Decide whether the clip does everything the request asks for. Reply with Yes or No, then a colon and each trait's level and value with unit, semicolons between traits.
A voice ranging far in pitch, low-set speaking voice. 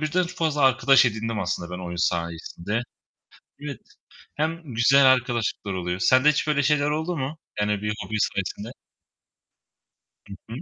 Yes: wide, 6.8 semitones; low, 120 Hz